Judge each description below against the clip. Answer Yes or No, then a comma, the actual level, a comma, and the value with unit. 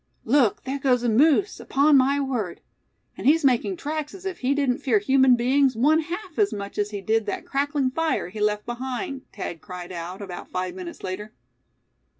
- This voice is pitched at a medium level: No, very high, 255 Hz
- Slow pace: No, average, 190 wpm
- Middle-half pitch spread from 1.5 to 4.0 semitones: No, wide, 5.5 semitones